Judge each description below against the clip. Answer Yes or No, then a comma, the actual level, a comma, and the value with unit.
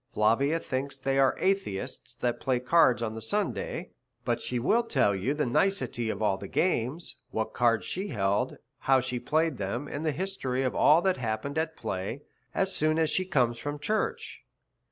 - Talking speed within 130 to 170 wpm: No, average, 190 wpm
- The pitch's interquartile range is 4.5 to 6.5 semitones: Yes, wide, 5.6 semitones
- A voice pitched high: No, low, 135 Hz